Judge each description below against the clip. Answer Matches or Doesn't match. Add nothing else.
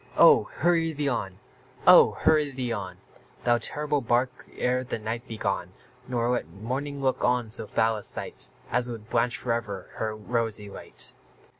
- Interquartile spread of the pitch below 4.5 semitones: Matches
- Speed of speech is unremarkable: Matches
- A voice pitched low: Matches